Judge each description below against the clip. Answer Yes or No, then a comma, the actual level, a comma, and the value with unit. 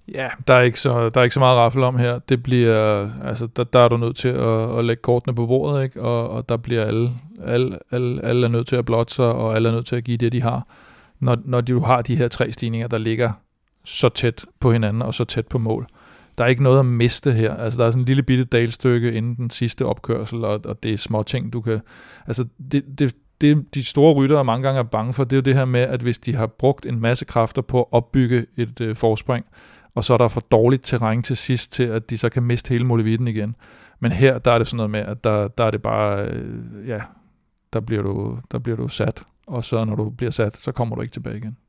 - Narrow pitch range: Yes, narrow, 2.0 semitones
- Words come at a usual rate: No, fast, 260 wpm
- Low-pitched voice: Yes, low, 120 Hz